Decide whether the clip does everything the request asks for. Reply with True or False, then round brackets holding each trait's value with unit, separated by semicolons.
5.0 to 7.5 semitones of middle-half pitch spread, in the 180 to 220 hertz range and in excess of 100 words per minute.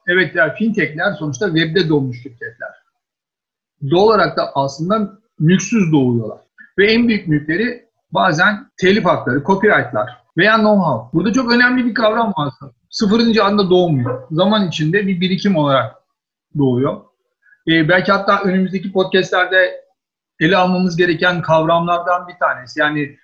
True (5.4 semitones; 185 Hz; 135 wpm)